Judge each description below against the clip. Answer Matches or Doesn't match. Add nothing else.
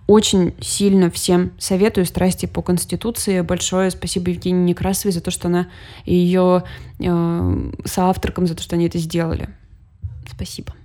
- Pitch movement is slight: Matches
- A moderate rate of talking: Matches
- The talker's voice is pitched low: Doesn't match